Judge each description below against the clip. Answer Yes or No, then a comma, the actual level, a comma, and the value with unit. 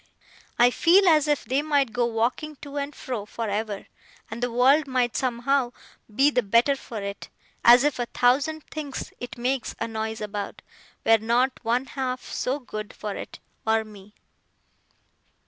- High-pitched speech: Yes, high, 245 Hz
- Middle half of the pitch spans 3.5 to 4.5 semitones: Yes, average, 3.8 semitones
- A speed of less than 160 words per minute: No, average, 165 wpm